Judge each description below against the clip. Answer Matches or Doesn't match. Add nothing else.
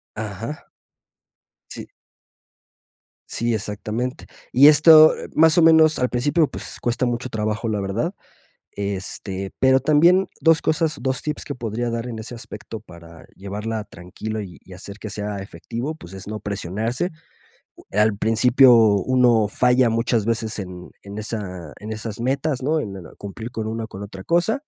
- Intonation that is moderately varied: Matches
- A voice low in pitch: Matches